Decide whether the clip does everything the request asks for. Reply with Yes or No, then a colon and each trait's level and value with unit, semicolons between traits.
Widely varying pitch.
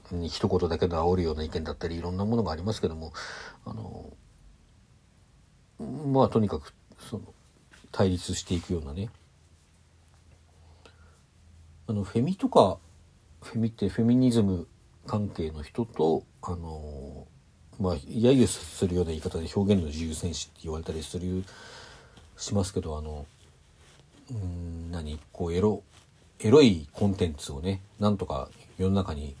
No: average, 4.2 semitones